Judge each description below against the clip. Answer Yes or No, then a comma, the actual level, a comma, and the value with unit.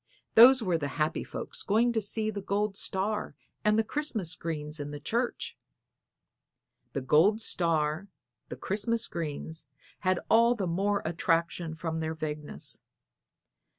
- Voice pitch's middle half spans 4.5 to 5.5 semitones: Yes, average, 5.2 semitones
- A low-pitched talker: No, medium, 185 Hz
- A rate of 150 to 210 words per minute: No, average, 140 wpm